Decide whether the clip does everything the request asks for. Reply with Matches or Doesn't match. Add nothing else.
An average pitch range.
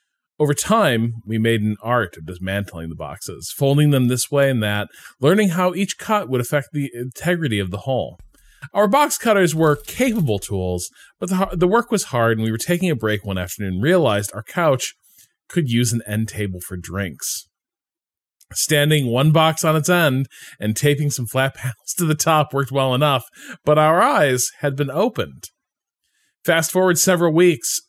Doesn't match